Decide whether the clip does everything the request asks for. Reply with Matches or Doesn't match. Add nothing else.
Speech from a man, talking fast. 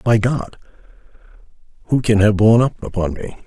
Doesn't match